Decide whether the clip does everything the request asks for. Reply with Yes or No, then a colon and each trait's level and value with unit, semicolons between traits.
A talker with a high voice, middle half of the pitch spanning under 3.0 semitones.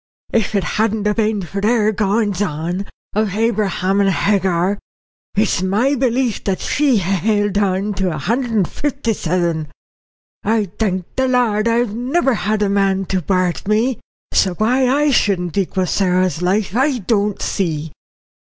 No: high, 205 Hz; average, 3.4 semitones